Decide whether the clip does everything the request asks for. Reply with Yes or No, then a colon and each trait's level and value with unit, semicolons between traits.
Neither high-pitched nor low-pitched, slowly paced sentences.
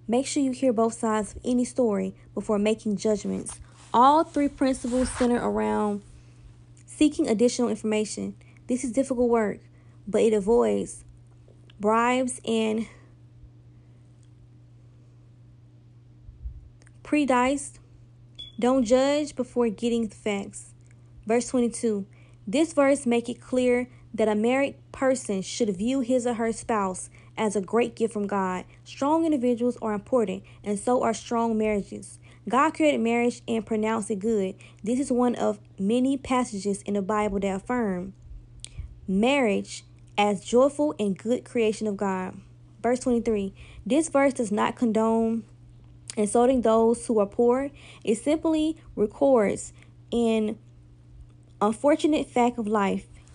No: high, 220 Hz; slow, 130 wpm